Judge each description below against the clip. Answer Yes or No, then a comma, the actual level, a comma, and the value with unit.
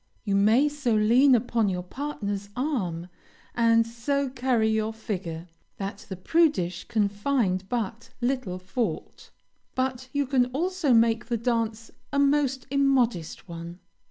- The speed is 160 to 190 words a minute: No, slow, 135 wpm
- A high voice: Yes, high, 230 Hz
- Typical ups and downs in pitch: Yes, average, 4.7 semitones